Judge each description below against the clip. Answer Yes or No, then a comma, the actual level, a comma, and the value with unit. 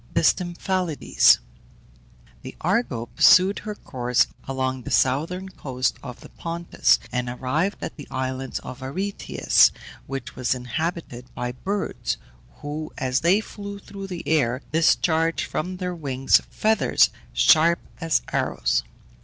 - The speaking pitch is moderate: Yes, medium, 155 Hz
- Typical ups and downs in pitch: No, wide, 6.0 semitones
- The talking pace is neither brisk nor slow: No, slow, 130 wpm